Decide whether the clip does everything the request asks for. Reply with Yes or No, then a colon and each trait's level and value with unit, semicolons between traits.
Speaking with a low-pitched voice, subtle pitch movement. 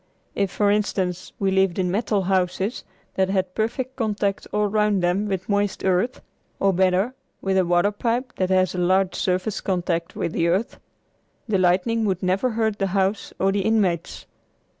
No: high, 195 Hz; narrow, 2.2 semitones